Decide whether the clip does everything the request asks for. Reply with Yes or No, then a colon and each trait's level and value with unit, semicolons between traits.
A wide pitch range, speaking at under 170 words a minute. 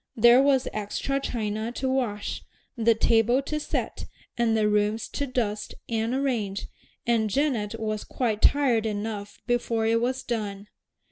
No: average, 3.0 semitones; average, 145 wpm